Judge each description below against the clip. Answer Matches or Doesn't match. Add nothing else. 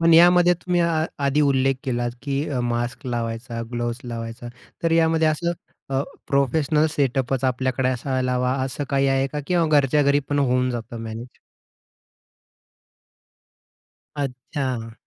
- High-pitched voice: Doesn't match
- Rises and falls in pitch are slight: Doesn't match